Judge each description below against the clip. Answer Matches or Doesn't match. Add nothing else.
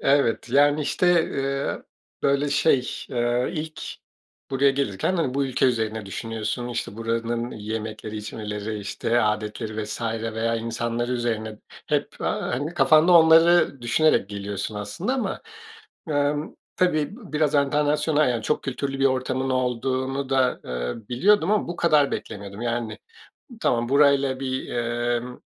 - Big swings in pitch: Doesn't match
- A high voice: Doesn't match